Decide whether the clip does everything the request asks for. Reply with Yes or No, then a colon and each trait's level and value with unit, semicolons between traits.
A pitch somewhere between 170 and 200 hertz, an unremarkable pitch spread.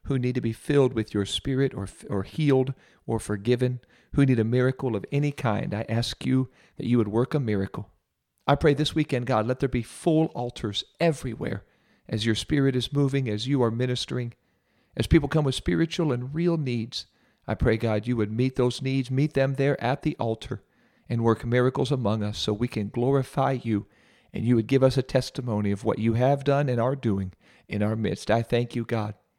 No: low, 125 Hz; average, 3.7 semitones